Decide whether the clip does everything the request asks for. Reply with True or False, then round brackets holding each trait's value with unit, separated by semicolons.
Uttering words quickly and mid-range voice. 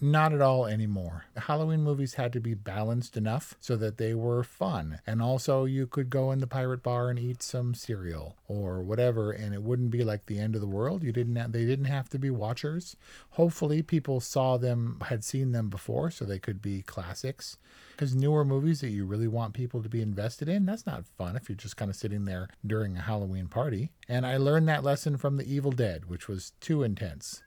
False (225 wpm; 120 Hz)